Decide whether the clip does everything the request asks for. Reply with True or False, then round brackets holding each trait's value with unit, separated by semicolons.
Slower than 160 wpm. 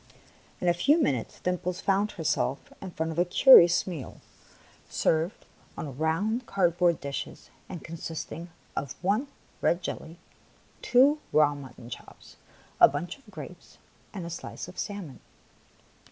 True (140 wpm)